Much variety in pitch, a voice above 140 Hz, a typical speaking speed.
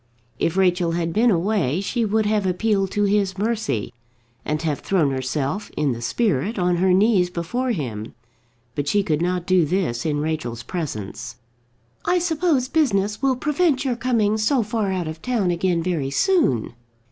Yes: wide, 6.0 semitones; medium, 185 Hz; average, 170 wpm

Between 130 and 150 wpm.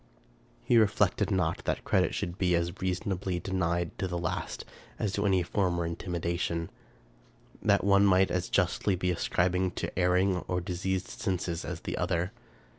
No: average, 160 wpm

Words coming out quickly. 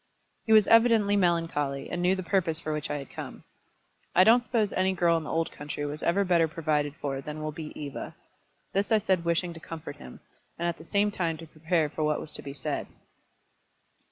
Yes: fast, 215 wpm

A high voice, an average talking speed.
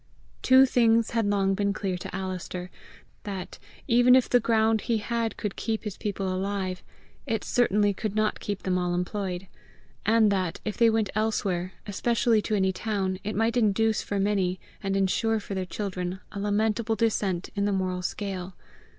Yes: high, 205 Hz; average, 175 wpm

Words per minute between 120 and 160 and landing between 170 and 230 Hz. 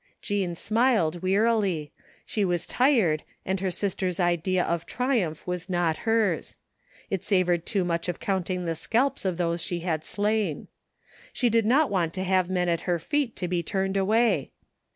No: average, 170 wpm; medium, 185 Hz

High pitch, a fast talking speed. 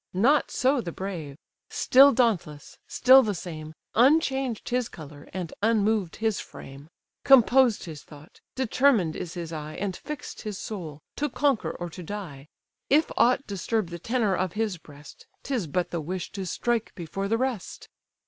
No: high, 200 Hz; average, 160 wpm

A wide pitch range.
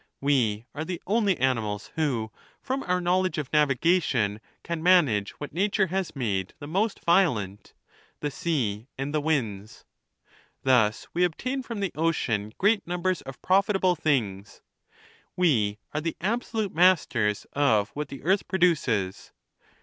Yes: wide, 8.3 semitones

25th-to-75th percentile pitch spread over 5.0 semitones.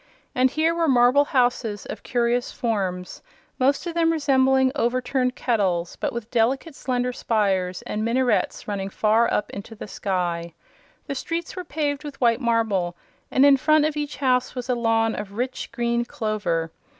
No: average, 4.3 semitones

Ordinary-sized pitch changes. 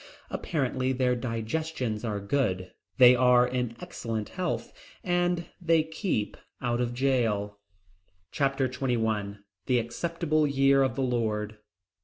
Yes: average, 3.7 semitones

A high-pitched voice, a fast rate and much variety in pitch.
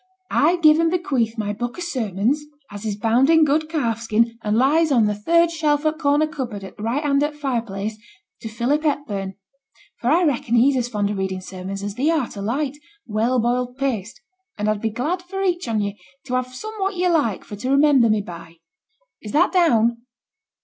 Yes: very high, 250 Hz; fast, 210 wpm; wide, 6.0 semitones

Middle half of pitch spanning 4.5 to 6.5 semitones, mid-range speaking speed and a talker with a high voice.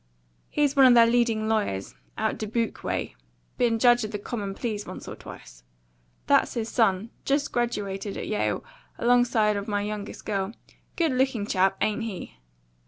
No: average, 2.9 semitones; average, 165 wpm; high, 220 Hz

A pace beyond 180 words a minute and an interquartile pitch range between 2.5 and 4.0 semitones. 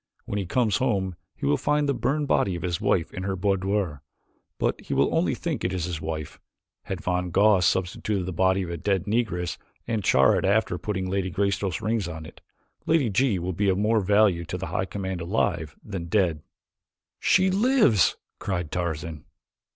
Yes: average, 190 wpm; average, 3.2 semitones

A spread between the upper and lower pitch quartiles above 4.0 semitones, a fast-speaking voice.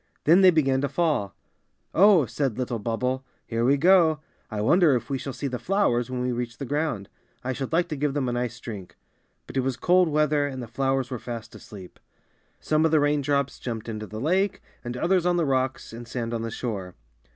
Yes: average, 4.4 semitones; fast, 220 wpm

